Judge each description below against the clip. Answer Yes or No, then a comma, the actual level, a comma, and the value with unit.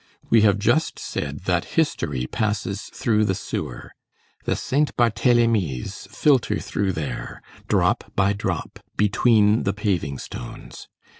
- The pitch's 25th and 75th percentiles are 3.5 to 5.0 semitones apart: Yes, average, 4.0 semitones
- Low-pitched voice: Yes, low, 105 Hz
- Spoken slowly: Yes, slow, 125 wpm